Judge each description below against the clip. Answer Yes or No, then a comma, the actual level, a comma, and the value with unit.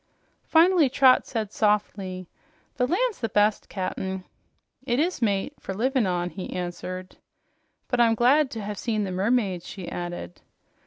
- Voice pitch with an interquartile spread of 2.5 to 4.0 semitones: No, average, 5.2 semitones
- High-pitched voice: Yes, high, 210 Hz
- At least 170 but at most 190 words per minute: No, average, 150 wpm